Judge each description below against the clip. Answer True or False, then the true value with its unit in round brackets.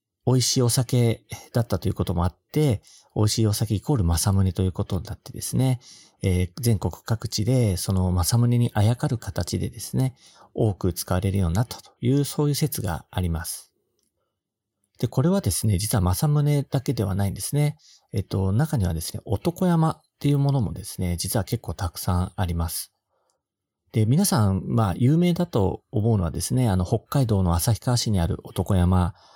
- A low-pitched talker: True (110 Hz)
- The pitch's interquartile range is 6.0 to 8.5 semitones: False (5.4 semitones)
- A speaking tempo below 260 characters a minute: False (360 characters per minute)